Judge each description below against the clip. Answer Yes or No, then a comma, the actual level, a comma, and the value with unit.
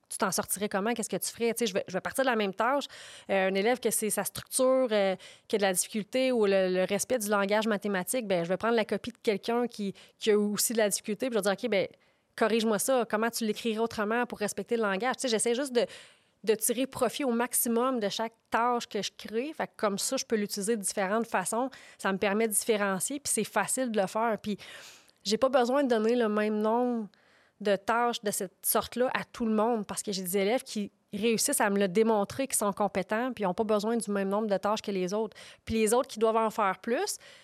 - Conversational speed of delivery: No, fast, 255 wpm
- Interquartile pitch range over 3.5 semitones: No, average, 2.8 semitones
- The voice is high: Yes, high, 220 Hz